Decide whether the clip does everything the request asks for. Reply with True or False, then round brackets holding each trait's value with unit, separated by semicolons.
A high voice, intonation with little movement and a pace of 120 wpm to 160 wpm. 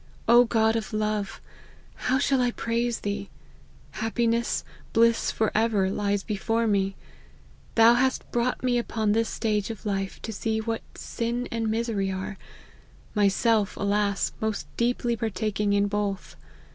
True (220 Hz; 2.3 semitones; 140 wpm)